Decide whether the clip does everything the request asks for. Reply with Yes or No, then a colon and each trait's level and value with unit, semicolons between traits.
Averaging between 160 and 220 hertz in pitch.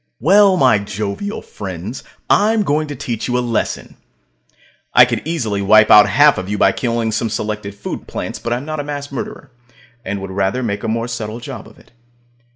No: low, 115 Hz